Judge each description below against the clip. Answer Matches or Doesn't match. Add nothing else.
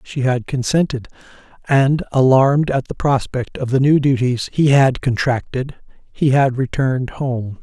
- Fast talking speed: Doesn't match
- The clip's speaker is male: Matches